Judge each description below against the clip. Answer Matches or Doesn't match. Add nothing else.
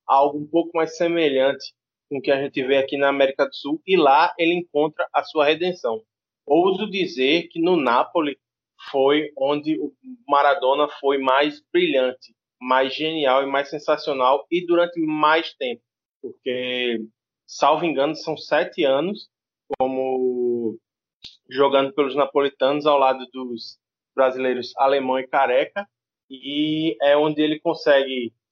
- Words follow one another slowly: Doesn't match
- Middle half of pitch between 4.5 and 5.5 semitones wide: Doesn't match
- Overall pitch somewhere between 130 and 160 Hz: Matches